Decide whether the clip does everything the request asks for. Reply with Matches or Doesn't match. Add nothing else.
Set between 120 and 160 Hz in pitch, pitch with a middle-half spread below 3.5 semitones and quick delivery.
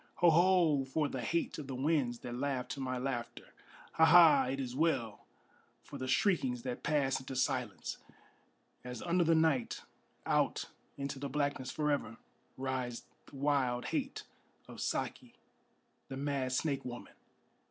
Doesn't match